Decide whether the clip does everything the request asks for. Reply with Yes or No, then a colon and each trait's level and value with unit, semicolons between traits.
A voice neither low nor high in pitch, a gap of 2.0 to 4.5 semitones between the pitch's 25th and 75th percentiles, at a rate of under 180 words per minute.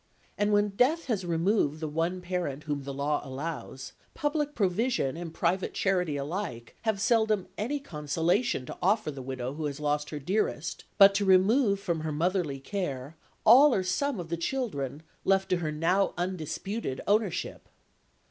No: medium, 180 Hz; wide, 5.5 semitones; average, 165 wpm